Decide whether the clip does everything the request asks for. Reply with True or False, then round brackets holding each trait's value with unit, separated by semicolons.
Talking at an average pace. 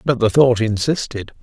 True (170 wpm)